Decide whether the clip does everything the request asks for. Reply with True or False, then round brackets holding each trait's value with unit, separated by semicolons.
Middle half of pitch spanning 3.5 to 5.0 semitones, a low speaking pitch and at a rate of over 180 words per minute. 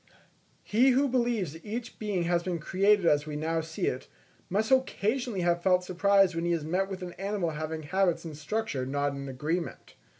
False (4.5 semitones; 180 Hz; 195 wpm)